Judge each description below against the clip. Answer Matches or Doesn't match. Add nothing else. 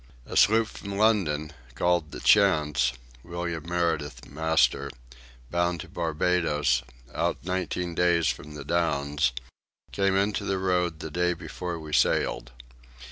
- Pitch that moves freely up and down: Doesn't match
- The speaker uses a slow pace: Matches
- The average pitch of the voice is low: Matches